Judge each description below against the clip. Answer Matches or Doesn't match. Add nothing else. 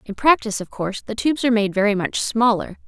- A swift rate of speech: Matches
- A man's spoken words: Doesn't match